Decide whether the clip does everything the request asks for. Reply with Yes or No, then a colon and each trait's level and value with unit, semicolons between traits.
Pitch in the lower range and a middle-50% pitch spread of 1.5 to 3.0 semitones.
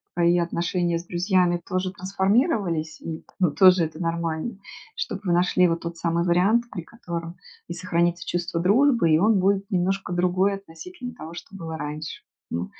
No: medium, 175 Hz; narrow, 2.4 semitones